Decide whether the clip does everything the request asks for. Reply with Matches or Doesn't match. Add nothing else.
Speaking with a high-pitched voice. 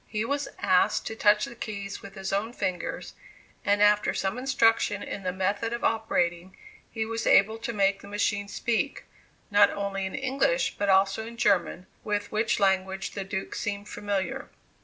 Matches